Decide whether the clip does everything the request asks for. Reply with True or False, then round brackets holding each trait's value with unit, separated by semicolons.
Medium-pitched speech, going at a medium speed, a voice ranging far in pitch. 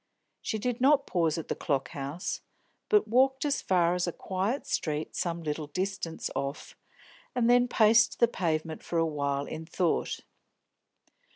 True (175 Hz; 160 wpm; 6.7 semitones)